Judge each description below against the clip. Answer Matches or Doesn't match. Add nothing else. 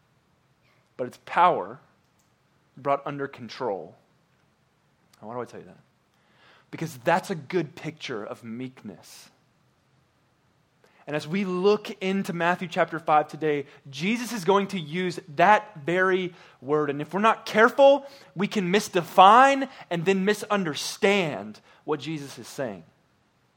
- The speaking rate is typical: Doesn't match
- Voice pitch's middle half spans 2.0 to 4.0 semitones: Doesn't match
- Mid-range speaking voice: Matches